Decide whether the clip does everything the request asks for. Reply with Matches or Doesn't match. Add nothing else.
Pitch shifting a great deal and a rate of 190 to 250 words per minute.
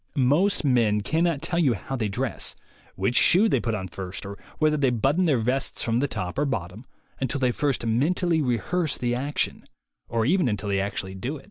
Matches